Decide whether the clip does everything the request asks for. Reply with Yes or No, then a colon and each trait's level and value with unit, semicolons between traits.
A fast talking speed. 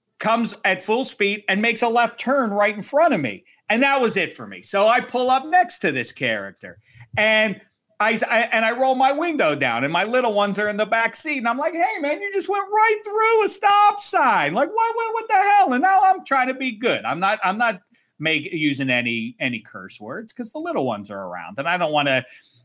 Yes: fast, 245 wpm